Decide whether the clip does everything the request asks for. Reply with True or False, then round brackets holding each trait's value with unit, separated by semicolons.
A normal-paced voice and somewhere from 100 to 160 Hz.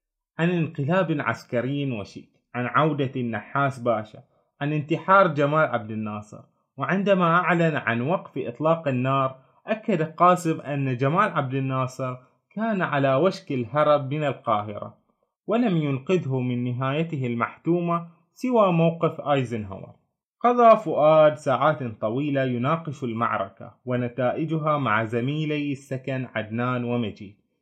True (110 wpm; 140 Hz)